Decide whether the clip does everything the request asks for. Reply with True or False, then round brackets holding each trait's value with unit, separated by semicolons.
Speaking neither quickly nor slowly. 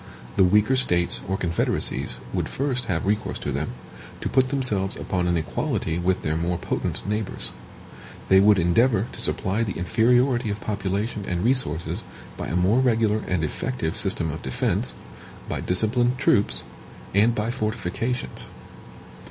True (150 wpm)